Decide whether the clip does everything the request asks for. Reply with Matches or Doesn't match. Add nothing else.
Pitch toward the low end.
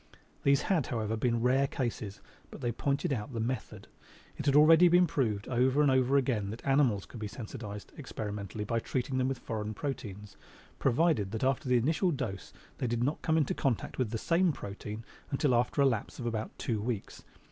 Matches